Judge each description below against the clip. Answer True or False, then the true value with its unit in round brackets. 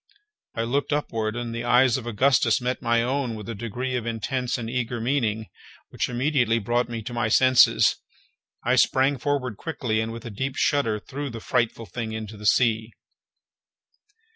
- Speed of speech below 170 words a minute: False (175 wpm)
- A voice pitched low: True (120 Hz)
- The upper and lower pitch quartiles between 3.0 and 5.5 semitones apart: False (2.4 semitones)